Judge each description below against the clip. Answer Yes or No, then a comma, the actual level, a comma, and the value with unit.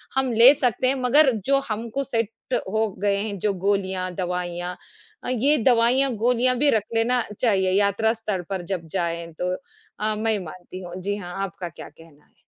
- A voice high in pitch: Yes, high, 210 Hz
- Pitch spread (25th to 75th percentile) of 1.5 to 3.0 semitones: No, average, 4.6 semitones